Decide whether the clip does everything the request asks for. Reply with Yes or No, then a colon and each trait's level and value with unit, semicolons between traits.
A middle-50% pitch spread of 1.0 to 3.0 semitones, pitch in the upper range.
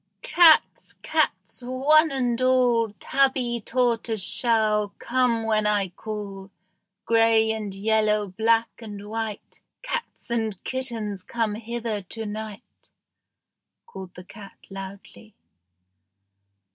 Yes: narrow, 2.6 semitones; high, 220 Hz